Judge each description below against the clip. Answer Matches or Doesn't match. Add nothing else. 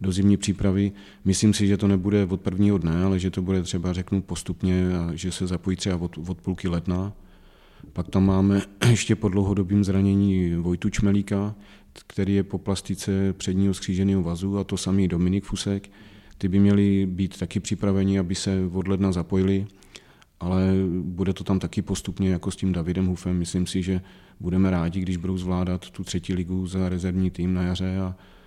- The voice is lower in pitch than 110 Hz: Matches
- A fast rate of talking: Matches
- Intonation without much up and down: Matches